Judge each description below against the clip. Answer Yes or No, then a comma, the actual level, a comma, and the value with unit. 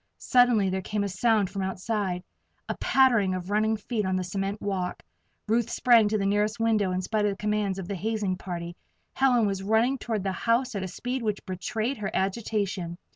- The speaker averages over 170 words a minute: Yes, average, 200 wpm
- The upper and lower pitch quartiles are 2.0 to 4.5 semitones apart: Yes, average, 2.9 semitones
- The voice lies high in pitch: Yes, high, 205 Hz